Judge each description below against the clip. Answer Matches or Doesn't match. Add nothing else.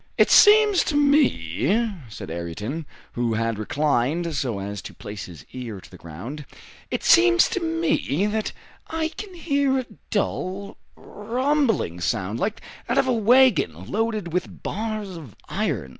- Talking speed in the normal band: Matches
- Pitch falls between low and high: Matches